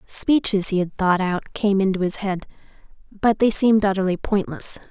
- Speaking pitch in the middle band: No, high, 195 Hz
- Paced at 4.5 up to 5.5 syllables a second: Yes, 4.9 syllables/s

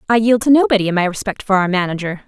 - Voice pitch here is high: Yes, high, 205 Hz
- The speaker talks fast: Yes, fast, 265 wpm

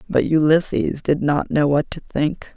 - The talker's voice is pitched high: No, medium, 150 Hz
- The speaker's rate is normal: Yes, average, 190 wpm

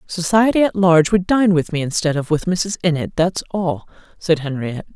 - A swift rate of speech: No, average, 195 wpm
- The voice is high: No, medium, 170 Hz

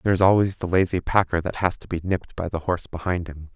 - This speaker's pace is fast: Yes, fast, 270 wpm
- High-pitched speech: No, very low, 90 Hz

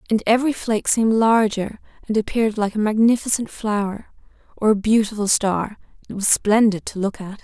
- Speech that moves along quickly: No, average, 160 wpm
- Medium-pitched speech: No, high, 215 Hz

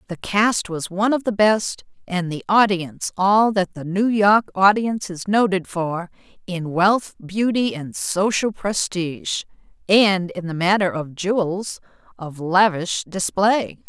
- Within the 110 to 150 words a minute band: Yes, average, 145 wpm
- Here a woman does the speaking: Yes, female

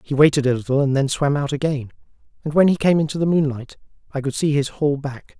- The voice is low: No, medium, 145 Hz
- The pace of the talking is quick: Yes, fast, 245 wpm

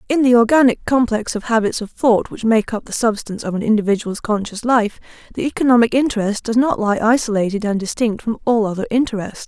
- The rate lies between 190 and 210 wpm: Yes, average, 195 wpm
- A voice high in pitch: Yes, high, 225 Hz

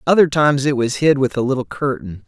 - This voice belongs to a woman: No, male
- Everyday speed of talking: No, fast, 240 wpm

